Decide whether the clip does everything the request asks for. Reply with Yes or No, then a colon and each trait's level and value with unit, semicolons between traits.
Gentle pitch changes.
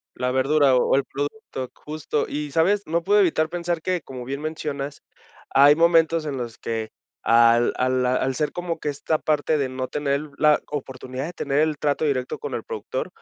No: average, 3.6 semitones